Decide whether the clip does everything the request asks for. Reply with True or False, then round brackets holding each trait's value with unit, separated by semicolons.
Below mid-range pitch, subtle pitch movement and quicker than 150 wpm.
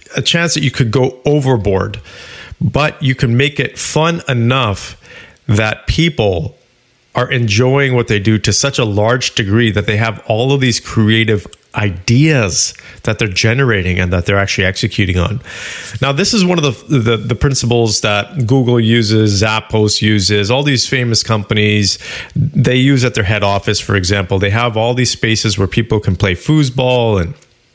False (115 Hz; 3.9 semitones; 175 wpm)